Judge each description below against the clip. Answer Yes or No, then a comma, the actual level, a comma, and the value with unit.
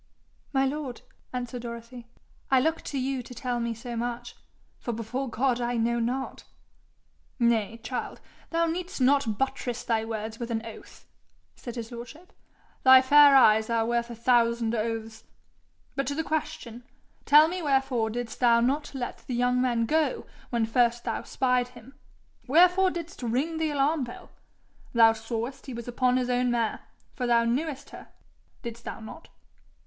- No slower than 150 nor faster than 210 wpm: Yes, average, 165 wpm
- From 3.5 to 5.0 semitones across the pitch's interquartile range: No, narrow, 2.5 semitones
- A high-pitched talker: Yes, high, 245 Hz